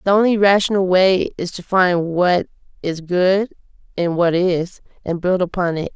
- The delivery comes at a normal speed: Yes, average, 170 wpm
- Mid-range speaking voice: Yes, medium, 180 Hz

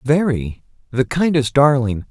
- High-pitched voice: No, low, 135 Hz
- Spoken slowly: Yes, slow, 85 wpm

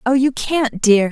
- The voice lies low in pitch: No, high, 245 Hz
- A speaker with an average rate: No, fast, 215 wpm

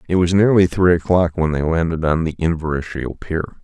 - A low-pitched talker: Yes, very low, 85 Hz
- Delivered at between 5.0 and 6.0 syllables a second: Yes, 5.7 syllables/s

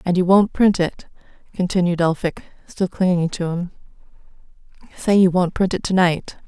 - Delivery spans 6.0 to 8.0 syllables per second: No, 5.1 syllables/s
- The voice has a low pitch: No, medium, 180 Hz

